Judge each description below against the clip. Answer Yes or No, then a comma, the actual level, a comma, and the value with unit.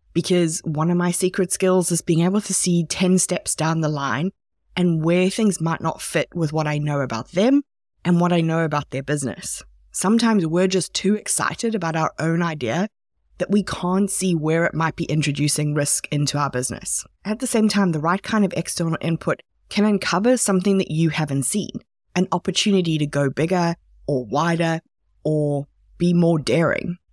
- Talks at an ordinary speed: Yes, average, 190 wpm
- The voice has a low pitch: No, medium, 170 Hz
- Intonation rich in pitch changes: No, average, 3.2 semitones